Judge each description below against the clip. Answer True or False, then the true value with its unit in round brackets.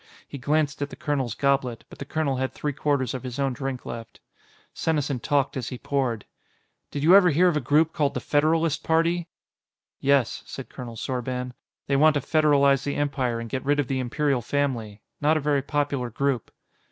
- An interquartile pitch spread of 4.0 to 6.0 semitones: False (2.6 semitones)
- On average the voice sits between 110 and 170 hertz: True (140 Hz)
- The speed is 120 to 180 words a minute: False (195 wpm)